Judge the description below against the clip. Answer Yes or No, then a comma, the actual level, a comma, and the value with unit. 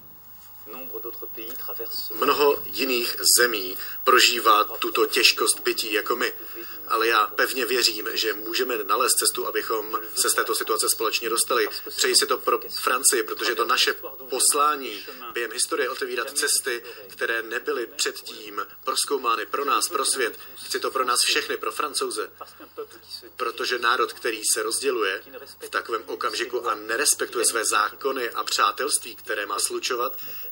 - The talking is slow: No, average, 135 wpm